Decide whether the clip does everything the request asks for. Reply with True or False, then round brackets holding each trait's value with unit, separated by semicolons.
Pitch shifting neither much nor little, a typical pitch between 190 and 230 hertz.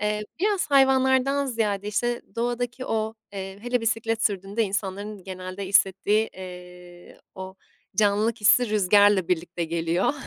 True (3.9 semitones; 210 Hz)